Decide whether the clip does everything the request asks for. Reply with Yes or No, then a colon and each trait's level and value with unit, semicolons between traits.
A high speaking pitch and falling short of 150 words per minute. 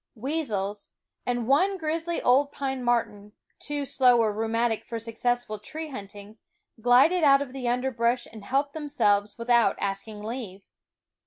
Yes: high, 240 Hz; average, 140 wpm